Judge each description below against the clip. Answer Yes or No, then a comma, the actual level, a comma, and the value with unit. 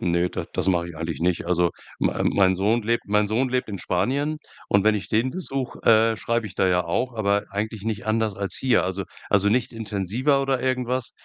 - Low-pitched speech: Yes, low, 110 Hz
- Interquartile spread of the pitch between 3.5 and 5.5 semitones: Yes, average, 4.4 semitones